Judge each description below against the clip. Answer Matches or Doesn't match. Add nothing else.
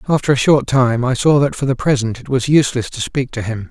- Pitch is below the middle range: Matches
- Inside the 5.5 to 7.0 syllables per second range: Matches